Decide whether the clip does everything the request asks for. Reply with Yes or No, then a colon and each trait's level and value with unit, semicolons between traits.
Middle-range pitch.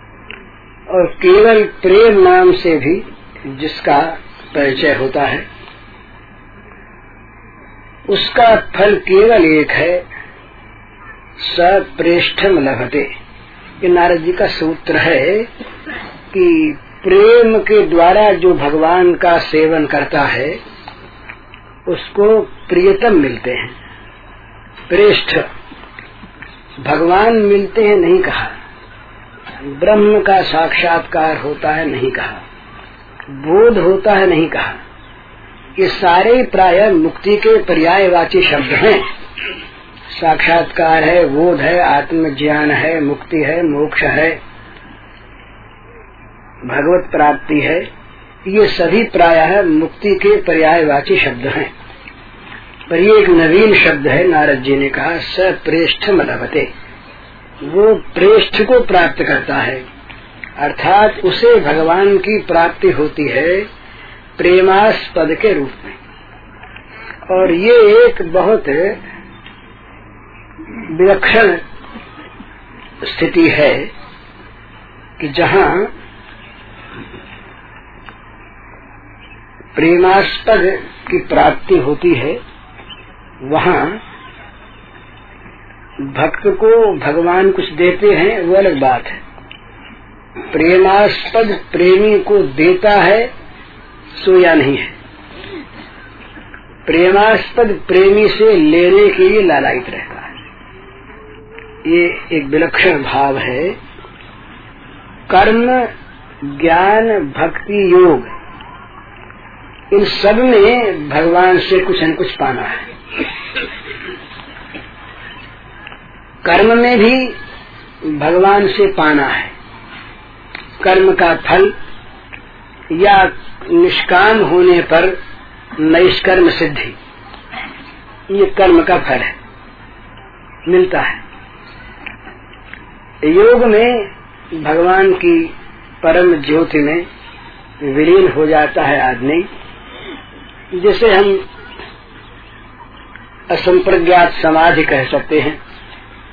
Yes: medium, 175 Hz